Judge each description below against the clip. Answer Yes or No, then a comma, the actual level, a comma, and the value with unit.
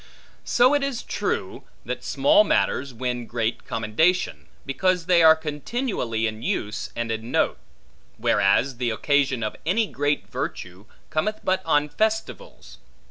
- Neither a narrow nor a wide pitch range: No, wide, 8.5 semitones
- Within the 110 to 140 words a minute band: Yes, slow, 135 wpm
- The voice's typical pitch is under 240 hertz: Yes, medium, 140 Hz